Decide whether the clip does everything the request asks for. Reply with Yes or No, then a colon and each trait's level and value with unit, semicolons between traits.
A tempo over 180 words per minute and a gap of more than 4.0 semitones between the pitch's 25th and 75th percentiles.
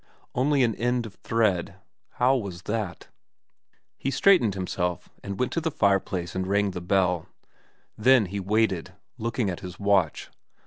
No: average, 150 wpm; average, 4.4 semitones